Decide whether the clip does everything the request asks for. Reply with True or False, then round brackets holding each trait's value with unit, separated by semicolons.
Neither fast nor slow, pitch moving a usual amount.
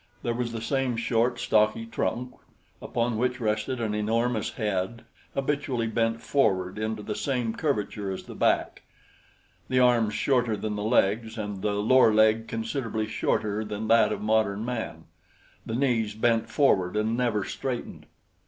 False (155 wpm; 2.3 semitones)